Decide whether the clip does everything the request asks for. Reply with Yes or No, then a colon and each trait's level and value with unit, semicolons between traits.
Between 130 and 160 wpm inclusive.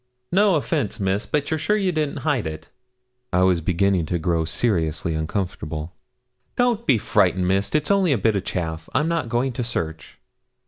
No: average, 180 wpm